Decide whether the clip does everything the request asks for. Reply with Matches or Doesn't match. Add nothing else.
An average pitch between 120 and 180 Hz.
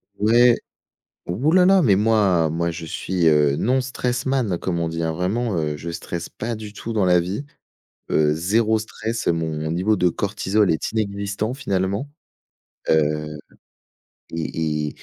Doesn't match